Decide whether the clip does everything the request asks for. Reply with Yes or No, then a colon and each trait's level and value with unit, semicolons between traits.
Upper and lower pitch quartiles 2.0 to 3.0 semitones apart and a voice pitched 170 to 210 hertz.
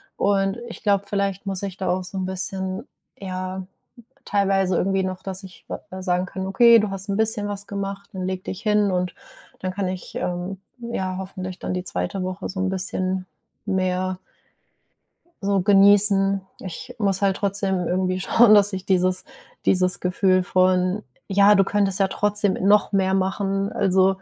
No: narrow, 1.3 semitones; high, 190 Hz